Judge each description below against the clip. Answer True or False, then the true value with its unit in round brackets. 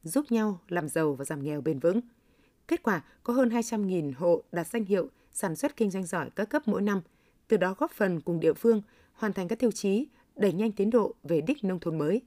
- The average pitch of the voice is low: False (205 Hz)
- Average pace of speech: True (235 wpm)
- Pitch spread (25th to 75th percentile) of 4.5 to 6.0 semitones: True (5.2 semitones)